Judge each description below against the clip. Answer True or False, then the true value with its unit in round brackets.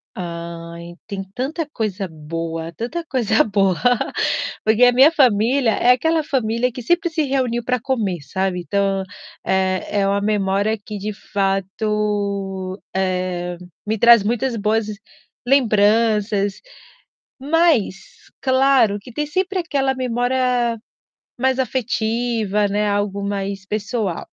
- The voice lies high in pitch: True (215 Hz)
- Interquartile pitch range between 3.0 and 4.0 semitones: False (4.4 semitones)